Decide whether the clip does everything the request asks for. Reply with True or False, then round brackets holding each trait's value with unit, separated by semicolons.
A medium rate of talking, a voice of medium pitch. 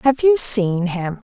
False (180 wpm; 220 Hz)